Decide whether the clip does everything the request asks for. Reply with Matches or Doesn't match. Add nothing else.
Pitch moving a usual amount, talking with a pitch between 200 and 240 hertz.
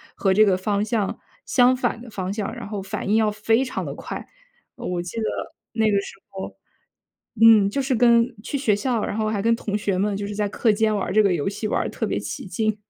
Doesn't match